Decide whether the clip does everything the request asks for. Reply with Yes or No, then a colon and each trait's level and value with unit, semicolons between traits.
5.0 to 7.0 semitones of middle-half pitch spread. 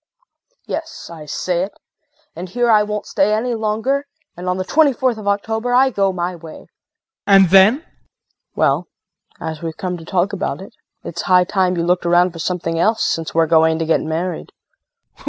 No: average, 4.2 semitones